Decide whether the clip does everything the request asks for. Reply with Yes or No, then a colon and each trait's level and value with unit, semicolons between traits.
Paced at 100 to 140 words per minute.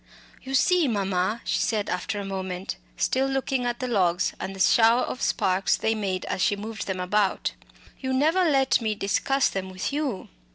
No: average, 190 wpm